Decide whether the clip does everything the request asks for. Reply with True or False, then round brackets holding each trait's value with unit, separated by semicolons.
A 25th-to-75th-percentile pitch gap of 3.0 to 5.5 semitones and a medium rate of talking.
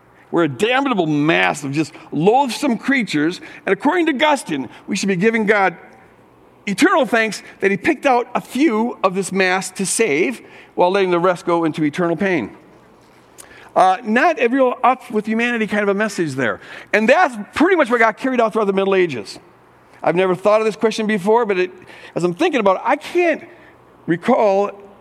True (4.9 semitones; 185 wpm)